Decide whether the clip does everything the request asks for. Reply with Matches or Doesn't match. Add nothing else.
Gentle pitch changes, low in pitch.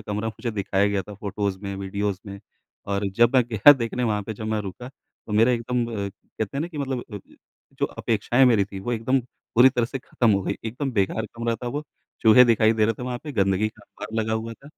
Doesn't match